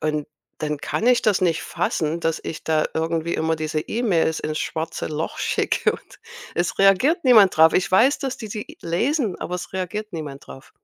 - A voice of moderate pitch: Yes, medium, 170 Hz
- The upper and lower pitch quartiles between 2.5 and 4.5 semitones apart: No, average, 5.1 semitones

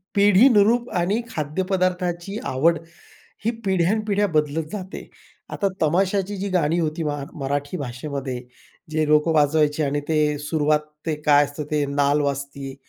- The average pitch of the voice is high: No, medium, 155 Hz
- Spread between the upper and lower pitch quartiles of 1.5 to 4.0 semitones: No, average, 4.4 semitones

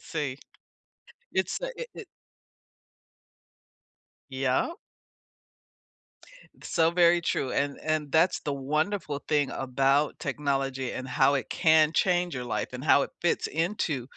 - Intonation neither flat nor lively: Yes, average, 3.4 semitones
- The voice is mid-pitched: Yes, medium, 145 Hz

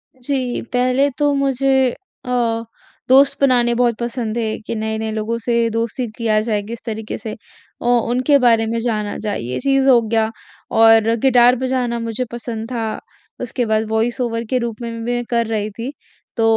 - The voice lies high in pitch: Yes, high, 235 Hz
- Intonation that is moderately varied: No, narrow, 2.1 semitones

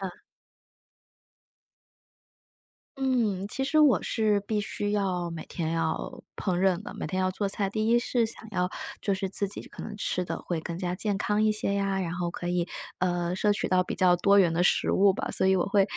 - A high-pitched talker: Yes, high, 195 Hz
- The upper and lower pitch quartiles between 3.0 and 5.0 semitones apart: No, narrow, 2.6 semitones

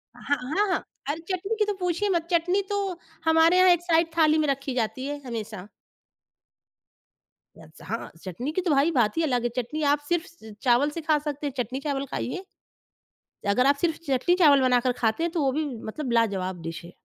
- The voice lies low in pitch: No, very high, 290 Hz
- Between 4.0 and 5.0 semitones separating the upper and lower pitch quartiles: No, wide, 5.5 semitones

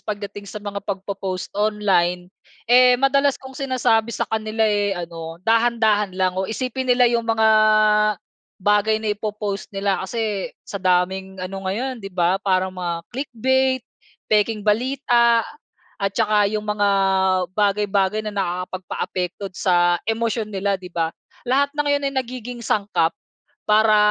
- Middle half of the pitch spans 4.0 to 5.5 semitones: No, average, 3.4 semitones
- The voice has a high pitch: Yes, high, 210 Hz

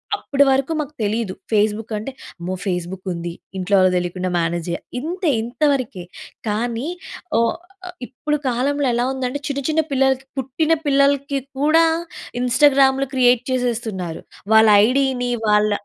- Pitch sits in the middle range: No, very high, 250 Hz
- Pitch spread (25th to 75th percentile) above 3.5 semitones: Yes, average, 5.0 semitones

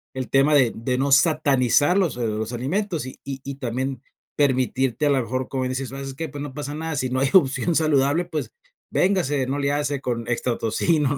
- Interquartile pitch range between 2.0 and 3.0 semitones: Yes, narrow, 2.4 semitones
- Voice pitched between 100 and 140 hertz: Yes, low, 135 Hz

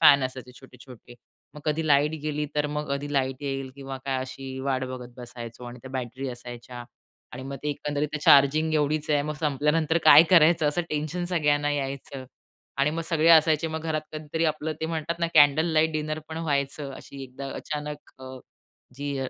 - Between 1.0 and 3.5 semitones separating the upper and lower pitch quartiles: Yes, narrow, 2.6 semitones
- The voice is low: No, medium, 145 Hz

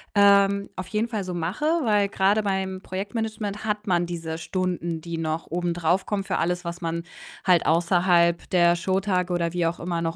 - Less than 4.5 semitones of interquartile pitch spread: Yes, average, 2.7 semitones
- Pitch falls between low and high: Yes, medium, 180 Hz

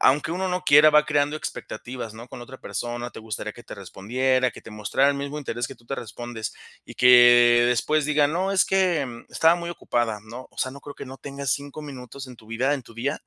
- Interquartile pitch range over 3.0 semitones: Yes, average, 3.6 semitones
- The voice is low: Yes, low, 130 Hz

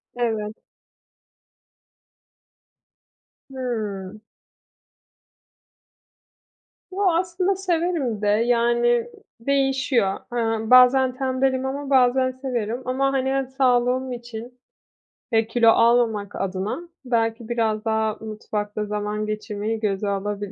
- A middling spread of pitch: Yes, average, 3.5 semitones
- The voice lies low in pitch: No, high, 235 Hz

